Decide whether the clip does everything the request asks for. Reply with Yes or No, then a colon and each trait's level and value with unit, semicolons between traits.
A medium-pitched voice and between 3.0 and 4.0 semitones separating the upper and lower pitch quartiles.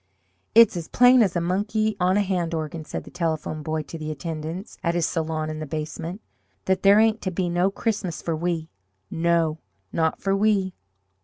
Yes: medium, 170 Hz; average, 3.6 semitones